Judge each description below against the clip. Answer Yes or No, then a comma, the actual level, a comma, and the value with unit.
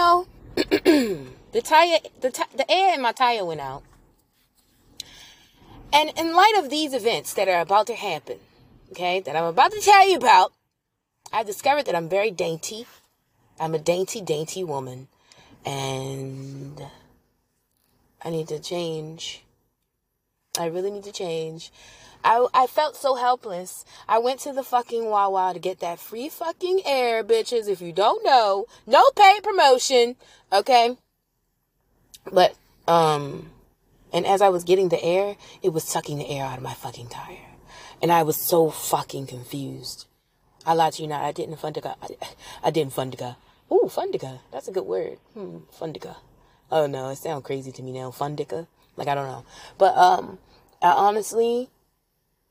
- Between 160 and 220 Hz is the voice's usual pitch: Yes, medium, 185 Hz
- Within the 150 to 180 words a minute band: Yes, average, 160 wpm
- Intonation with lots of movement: Yes, wide, 8.9 semitones